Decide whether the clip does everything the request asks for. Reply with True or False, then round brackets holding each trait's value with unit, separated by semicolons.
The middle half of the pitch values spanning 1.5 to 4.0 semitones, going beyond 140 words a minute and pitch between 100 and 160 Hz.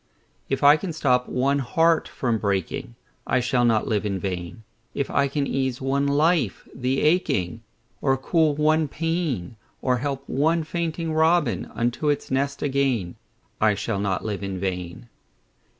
False (5.6 semitones; 155 wpm; 135 Hz)